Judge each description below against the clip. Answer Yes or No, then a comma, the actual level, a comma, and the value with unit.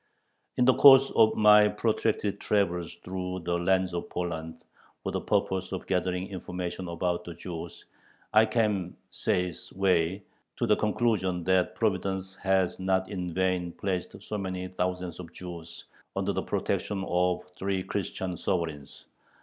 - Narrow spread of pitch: Yes, narrow, 1.8 semitones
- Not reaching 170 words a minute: Yes, average, 145 wpm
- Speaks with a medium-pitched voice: No, very low, 95 Hz